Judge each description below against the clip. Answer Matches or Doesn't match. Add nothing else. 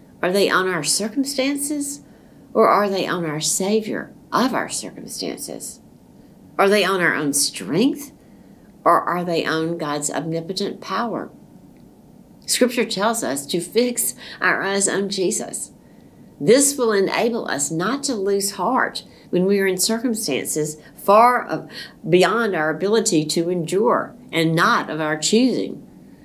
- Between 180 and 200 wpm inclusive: Doesn't match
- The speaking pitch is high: Matches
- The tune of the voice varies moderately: Doesn't match